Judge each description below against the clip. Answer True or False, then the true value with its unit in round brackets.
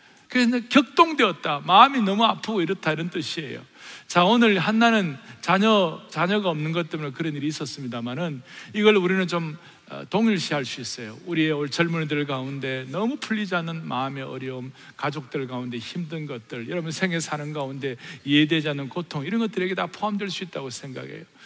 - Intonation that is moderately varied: False (5.7 semitones)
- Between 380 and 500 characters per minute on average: True (385 characters per minute)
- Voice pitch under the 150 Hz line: False (165 Hz)